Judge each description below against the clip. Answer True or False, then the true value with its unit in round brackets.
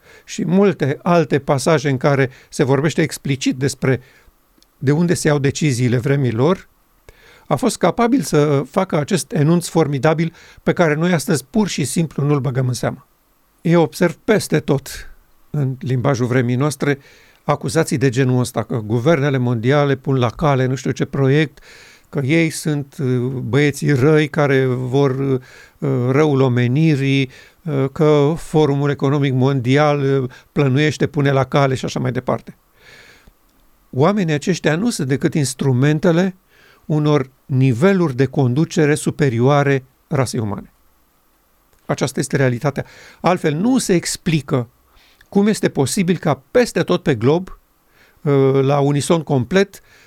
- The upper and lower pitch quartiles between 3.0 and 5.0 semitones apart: True (3.5 semitones)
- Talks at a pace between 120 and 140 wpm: True (130 wpm)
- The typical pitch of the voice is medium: True (145 Hz)